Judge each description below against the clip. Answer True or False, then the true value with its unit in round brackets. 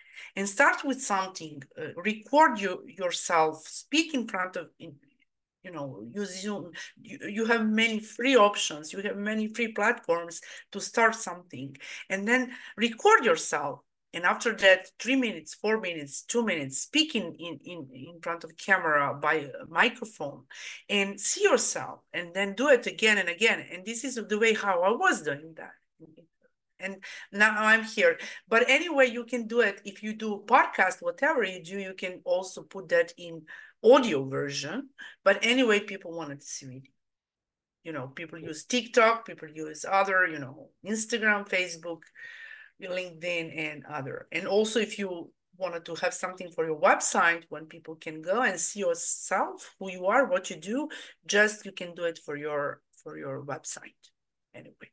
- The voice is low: False (195 Hz)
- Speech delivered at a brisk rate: False (170 wpm)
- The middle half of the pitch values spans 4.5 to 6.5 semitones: True (5.6 semitones)